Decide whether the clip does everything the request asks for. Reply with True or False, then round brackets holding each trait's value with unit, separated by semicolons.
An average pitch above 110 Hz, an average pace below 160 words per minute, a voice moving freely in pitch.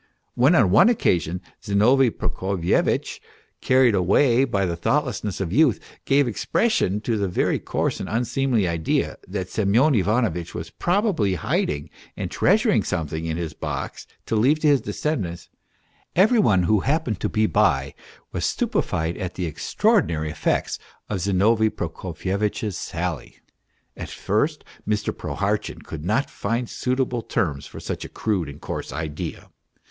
False (100 Hz; 145 wpm; 6.6 semitones)